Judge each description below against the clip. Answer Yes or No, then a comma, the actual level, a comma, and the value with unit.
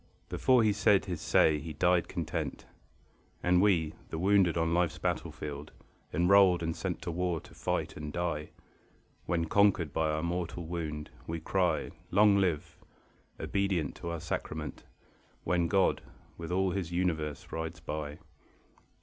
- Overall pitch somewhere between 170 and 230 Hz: No, very low, 85 Hz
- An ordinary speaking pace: Yes, average, 145 wpm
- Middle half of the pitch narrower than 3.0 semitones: Yes, narrow, 2.6 semitones